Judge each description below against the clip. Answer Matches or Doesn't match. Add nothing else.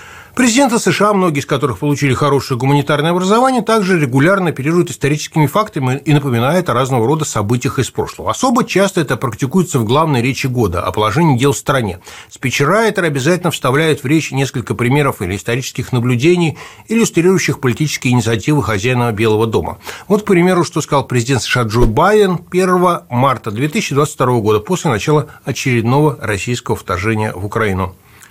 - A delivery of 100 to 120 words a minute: Doesn't match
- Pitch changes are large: Matches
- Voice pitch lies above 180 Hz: Doesn't match